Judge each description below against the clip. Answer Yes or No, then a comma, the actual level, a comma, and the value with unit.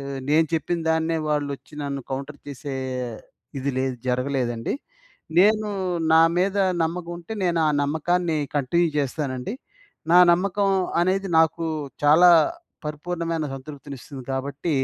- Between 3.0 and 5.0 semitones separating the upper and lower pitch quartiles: Yes, average, 3.9 semitones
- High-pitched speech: No, medium, 155 Hz